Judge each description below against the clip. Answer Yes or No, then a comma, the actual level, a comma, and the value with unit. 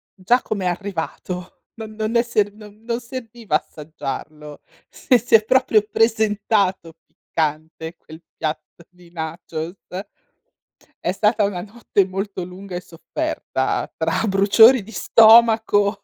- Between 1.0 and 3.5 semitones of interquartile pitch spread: No, average, 4.2 semitones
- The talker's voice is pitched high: Yes, high, 200 Hz